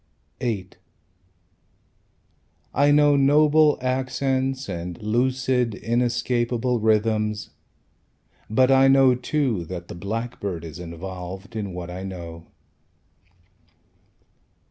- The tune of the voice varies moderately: No, wide, 5.7 semitones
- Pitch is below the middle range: Yes, low, 115 Hz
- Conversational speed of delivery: No, slow, 90 wpm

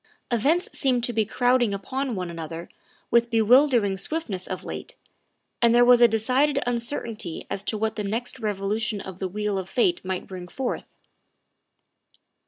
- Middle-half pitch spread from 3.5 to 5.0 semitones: Yes, average, 3.9 semitones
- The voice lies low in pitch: No, high, 225 Hz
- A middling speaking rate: Yes, average, 160 wpm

